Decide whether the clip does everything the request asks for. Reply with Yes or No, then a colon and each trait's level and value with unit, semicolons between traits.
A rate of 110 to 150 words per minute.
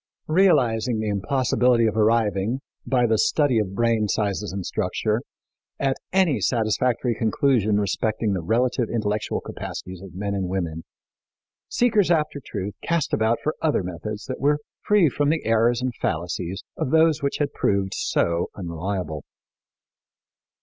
Yes: average, 145 wpm